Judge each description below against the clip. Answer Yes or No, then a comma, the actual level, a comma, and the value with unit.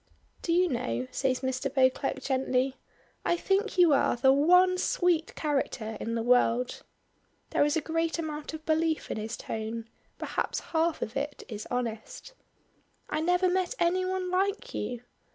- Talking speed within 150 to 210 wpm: Yes, average, 160 wpm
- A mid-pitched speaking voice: No, very high, 295 Hz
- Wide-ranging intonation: Yes, wide, 5.8 semitones